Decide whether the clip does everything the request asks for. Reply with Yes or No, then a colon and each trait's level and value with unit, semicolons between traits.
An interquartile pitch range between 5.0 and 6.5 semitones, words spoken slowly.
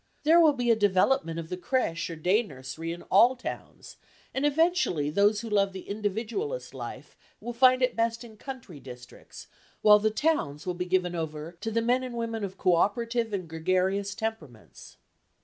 No: wide, 5.6 semitones; average, 185 wpm